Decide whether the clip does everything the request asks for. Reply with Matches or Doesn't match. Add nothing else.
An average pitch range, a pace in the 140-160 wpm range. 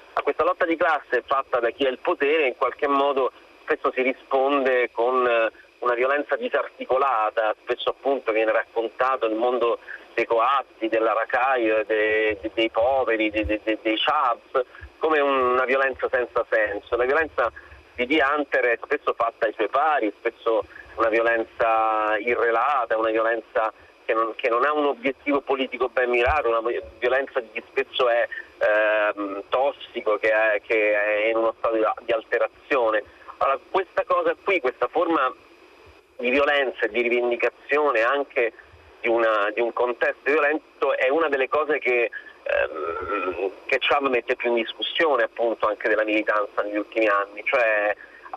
Matches